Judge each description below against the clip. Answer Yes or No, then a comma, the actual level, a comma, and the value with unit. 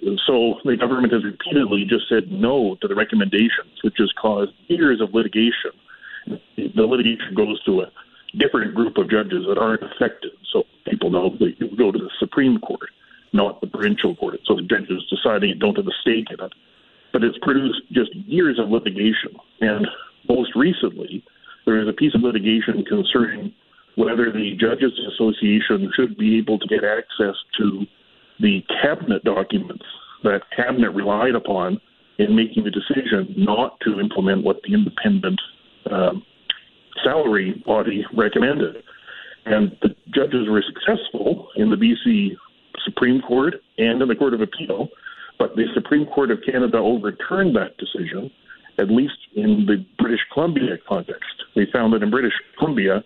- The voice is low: Yes, low, 125 Hz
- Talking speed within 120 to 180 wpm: Yes, average, 160 wpm